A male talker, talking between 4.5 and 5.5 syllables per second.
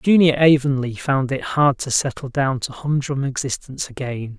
Yes: male; 4.8 syllables/s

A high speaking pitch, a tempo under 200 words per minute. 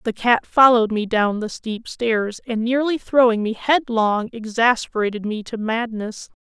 Yes: high, 230 Hz; average, 160 wpm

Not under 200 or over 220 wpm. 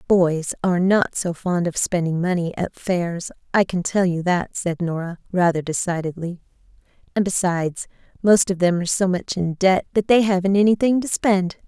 No: average, 180 wpm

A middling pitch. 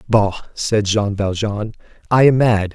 No: low, 105 Hz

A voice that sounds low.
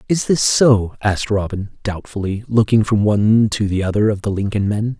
Yes: low, 105 Hz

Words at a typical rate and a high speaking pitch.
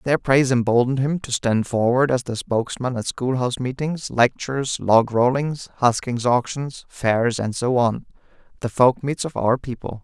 No: average, 160 wpm; low, 125 Hz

